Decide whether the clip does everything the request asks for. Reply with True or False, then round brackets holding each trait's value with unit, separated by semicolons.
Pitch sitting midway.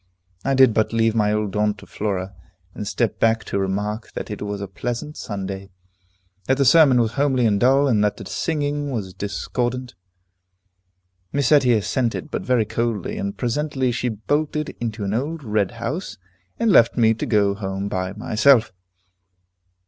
False (115 Hz)